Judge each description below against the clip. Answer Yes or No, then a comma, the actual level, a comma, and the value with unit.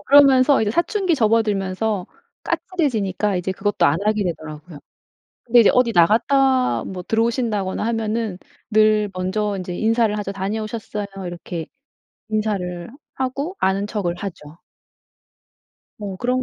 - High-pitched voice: Yes, high, 210 Hz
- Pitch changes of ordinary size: Yes, average, 3.8 semitones